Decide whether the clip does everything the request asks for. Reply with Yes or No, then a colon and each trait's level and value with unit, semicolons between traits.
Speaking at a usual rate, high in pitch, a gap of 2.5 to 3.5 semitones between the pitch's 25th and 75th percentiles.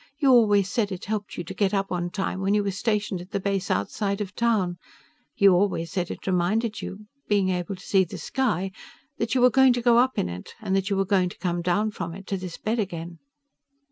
No: fast, 240 wpm; high, 195 Hz; average, 2.8 semitones